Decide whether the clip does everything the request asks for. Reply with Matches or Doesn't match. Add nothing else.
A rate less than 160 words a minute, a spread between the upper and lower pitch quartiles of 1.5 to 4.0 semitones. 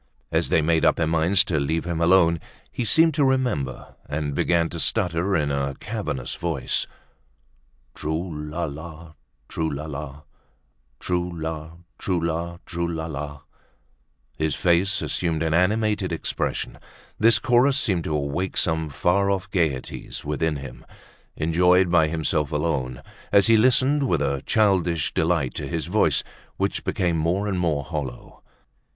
Matches